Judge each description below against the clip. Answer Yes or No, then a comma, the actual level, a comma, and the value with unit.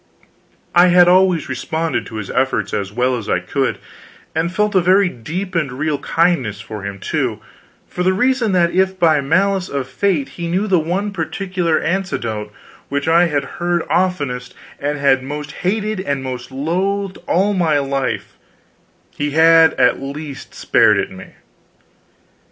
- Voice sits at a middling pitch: Yes, medium, 165 Hz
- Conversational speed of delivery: Yes, average, 160 wpm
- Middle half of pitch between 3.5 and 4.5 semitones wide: No, average, 5.3 semitones